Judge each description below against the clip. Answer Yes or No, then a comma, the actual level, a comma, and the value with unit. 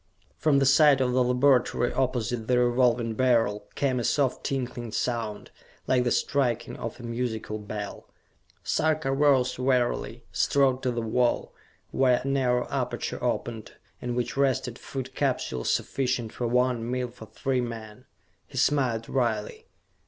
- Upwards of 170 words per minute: No, average, 145 wpm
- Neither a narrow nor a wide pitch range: No, narrow, 2.0 semitones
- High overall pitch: No, low, 125 Hz